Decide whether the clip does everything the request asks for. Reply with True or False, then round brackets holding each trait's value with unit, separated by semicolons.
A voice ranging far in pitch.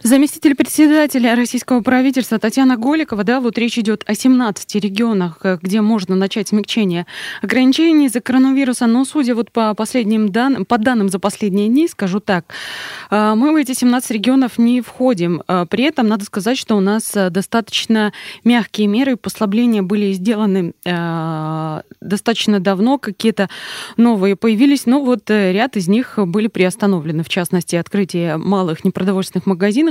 False (4.1 semitones)